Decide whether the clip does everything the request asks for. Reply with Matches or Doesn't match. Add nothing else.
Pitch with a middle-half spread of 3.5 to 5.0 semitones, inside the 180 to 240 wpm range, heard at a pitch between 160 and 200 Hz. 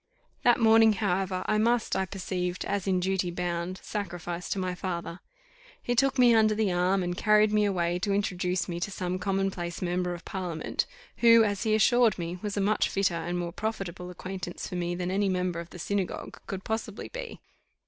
Doesn't match